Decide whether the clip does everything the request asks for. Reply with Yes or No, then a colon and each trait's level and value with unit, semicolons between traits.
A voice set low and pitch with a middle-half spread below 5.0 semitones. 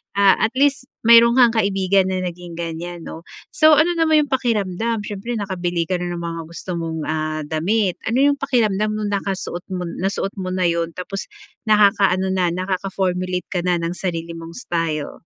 No: medium, 185 Hz; average, 3.9 semitones